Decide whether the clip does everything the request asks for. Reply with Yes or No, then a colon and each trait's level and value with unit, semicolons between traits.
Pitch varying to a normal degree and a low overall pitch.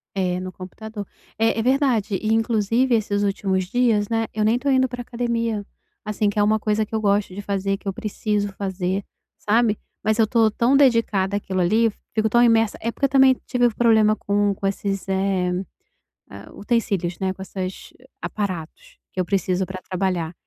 No: average, 3.0 semitones; high, 210 Hz